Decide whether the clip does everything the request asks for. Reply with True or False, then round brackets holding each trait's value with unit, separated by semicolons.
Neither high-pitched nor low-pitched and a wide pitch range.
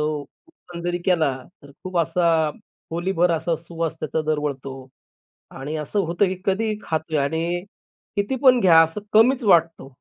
False (165 Hz; 3.2 semitones)